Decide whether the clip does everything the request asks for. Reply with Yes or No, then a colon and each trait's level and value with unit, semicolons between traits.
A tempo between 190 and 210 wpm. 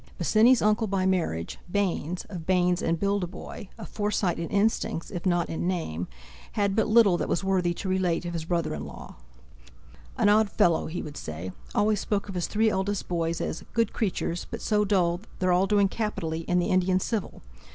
Yes: average, 195 wpm